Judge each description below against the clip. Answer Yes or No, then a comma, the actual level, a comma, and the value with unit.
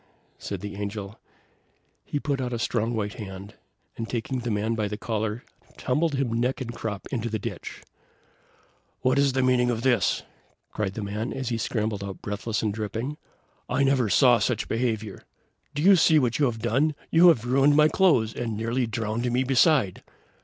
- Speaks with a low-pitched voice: Yes, low, 120 Hz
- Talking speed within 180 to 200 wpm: Yes, average, 185 wpm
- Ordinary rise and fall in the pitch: Yes, average, 3.5 semitones